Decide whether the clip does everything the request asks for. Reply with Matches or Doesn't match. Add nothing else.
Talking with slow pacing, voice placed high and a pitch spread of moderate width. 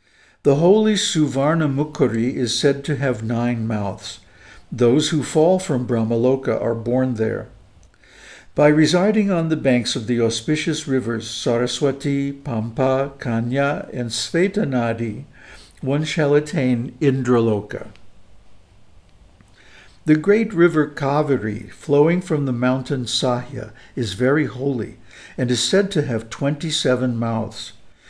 Doesn't match